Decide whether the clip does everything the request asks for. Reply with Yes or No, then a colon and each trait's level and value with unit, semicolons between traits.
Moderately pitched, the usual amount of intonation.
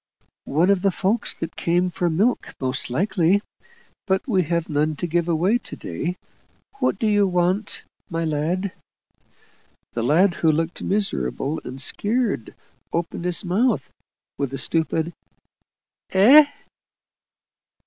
Yes: medium, 175 Hz; average, 3.9 semitones